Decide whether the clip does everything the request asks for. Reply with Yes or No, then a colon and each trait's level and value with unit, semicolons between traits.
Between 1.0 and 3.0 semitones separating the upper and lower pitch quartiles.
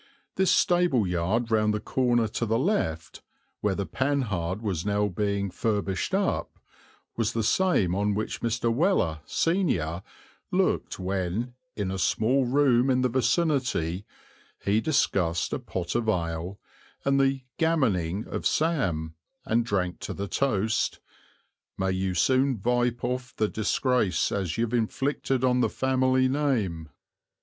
No: wide, 5.5 semitones